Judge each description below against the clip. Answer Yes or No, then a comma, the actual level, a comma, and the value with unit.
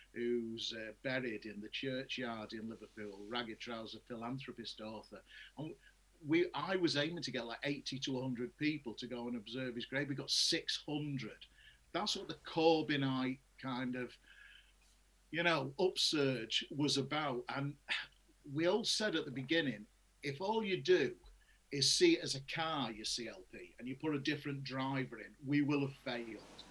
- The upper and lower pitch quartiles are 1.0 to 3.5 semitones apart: No, average, 4.1 semitones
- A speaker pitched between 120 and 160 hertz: Yes, low, 135 Hz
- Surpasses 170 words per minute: No, average, 165 wpm